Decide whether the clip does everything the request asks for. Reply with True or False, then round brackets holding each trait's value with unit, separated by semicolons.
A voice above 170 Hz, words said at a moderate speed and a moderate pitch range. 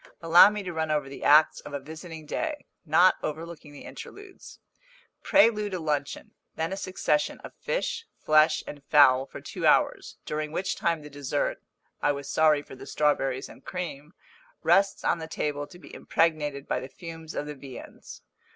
False (155 Hz; 180 wpm; 3.3 semitones)